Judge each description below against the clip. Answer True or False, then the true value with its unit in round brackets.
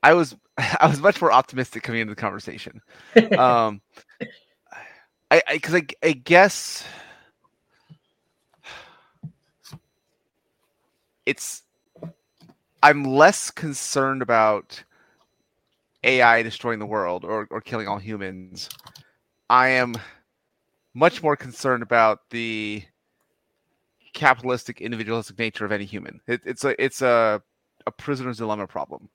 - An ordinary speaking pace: False (110 wpm)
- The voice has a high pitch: False (120 Hz)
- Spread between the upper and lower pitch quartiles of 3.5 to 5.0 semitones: True (4.1 semitones)